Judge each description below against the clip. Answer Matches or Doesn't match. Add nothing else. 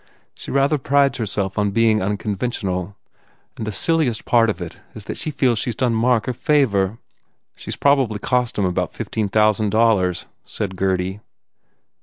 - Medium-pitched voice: Doesn't match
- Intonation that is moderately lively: Matches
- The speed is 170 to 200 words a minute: Matches